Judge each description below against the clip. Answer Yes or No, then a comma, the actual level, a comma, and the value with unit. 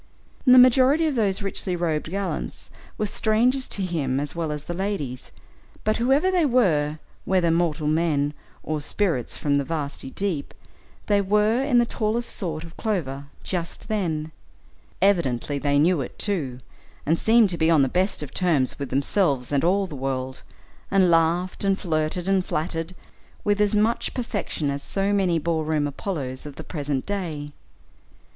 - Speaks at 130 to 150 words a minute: No, average, 165 wpm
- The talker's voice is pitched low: No, medium, 170 Hz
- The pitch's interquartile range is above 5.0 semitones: Yes, wide, 5.6 semitones